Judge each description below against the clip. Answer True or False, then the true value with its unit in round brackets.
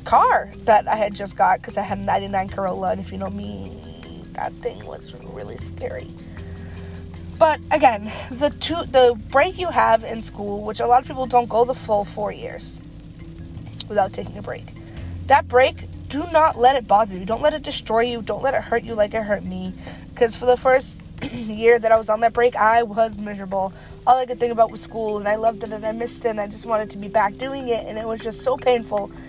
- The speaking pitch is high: True (220 Hz)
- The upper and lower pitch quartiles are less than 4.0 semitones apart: False (4.5 semitones)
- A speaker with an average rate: False (230 wpm)